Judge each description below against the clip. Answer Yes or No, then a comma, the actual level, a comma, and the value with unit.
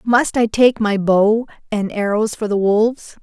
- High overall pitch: Yes, high, 215 Hz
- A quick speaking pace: No, average, 185 wpm